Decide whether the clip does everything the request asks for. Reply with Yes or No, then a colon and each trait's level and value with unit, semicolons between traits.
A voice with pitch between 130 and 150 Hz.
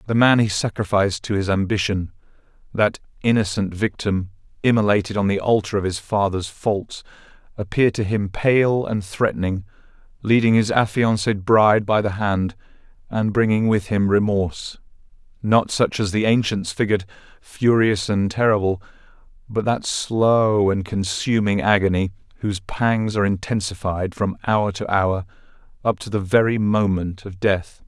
No: low, 100 Hz